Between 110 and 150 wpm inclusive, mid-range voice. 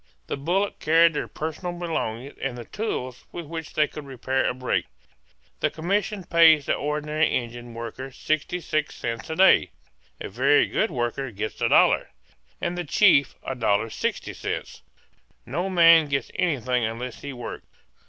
Yes: average, 145 wpm; medium, 150 Hz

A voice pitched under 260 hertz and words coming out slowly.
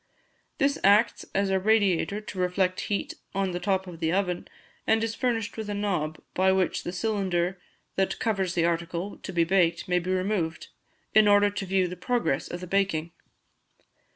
No: high, 190 Hz; average, 180 wpm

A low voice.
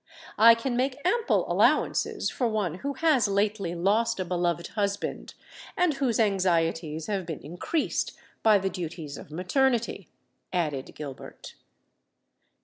No: high, 200 Hz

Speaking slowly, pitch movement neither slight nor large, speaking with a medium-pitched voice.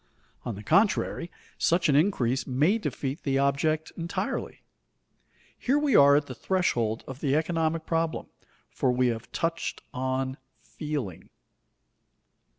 Yes: slow, 130 wpm; average, 4.2 semitones; medium, 145 Hz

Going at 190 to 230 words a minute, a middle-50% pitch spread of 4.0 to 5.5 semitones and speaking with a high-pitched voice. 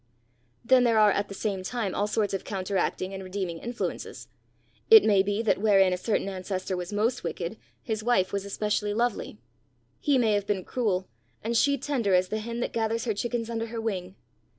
No: average, 195 wpm; average, 3.2 semitones; high, 210 Hz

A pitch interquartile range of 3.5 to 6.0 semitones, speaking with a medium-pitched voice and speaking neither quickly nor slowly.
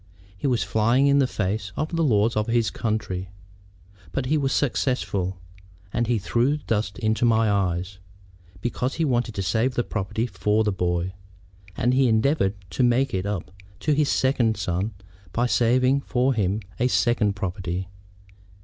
No: average, 4.5 semitones; low, 110 Hz; average, 165 wpm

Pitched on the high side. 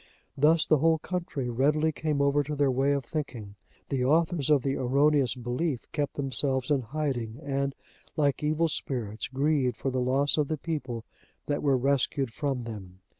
No: medium, 140 Hz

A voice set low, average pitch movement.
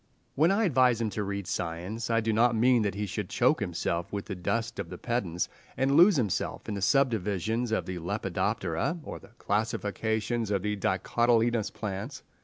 Yes: low, 110 Hz; average, 3.3 semitones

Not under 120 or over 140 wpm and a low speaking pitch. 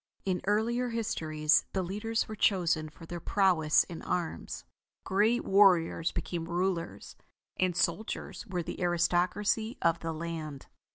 No: slow, 135 wpm; medium, 180 Hz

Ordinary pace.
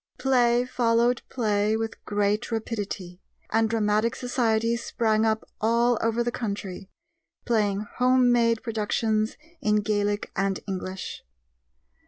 No: slow, 115 wpm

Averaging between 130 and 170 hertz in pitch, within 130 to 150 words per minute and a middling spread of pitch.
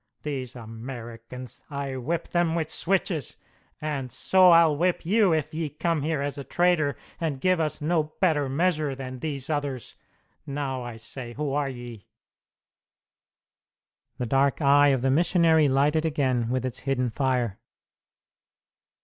Yes: medium, 140 Hz; average, 145 wpm; average, 3.8 semitones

